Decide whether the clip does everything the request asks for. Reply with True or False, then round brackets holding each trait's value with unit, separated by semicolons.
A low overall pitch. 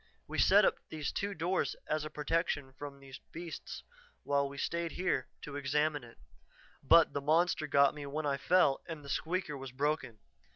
False (150 Hz)